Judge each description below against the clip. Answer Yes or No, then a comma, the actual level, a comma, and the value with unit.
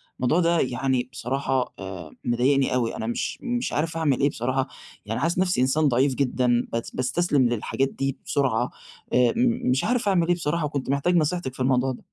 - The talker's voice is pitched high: No, low, 135 Hz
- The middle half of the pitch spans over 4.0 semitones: Yes, average, 4.7 semitones